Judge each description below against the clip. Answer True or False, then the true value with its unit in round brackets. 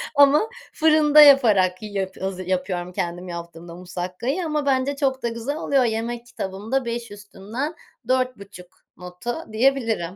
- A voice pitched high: True (225 Hz)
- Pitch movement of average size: False (6.7 semitones)